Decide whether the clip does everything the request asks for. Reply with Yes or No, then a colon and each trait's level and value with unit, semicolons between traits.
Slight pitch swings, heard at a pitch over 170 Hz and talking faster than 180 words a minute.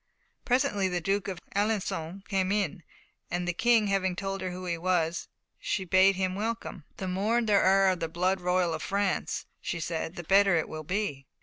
Yes: narrow, 2.2 semitones; high, 190 Hz; average, 195 wpm